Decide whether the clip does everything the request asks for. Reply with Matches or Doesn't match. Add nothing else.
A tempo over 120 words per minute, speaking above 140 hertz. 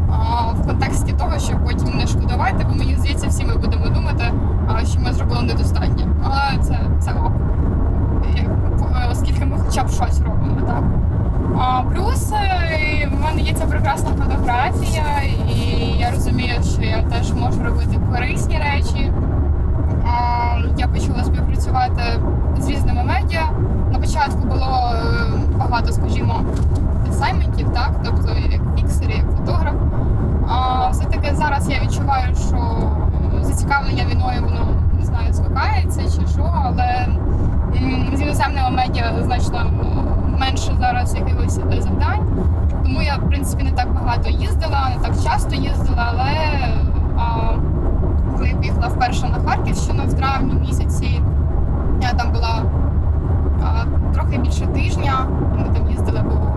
Doesn't match